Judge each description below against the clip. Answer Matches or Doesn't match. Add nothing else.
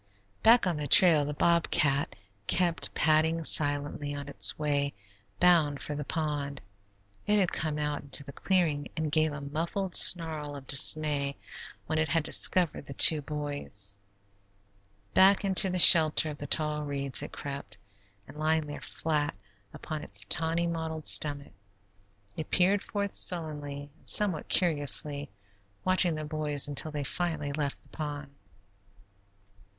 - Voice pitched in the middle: Matches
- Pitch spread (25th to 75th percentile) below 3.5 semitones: Matches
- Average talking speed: Matches